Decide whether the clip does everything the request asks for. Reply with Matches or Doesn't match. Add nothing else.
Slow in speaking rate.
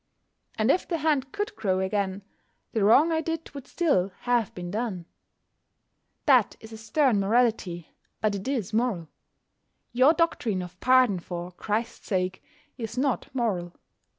Doesn't match